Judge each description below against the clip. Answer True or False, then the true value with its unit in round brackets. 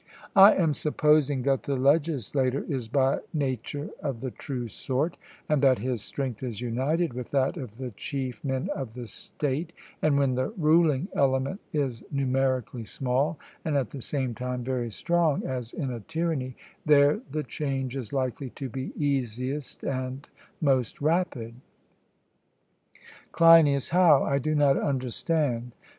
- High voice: False (135 Hz)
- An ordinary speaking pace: True (150 wpm)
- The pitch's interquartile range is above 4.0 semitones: False (2.9 semitones)